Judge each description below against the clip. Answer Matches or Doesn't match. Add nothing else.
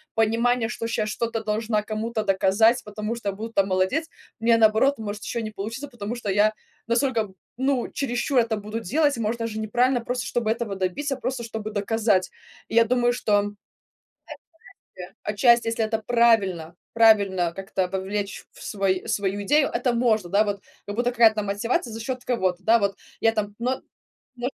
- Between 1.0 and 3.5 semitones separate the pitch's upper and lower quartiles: Matches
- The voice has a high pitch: Matches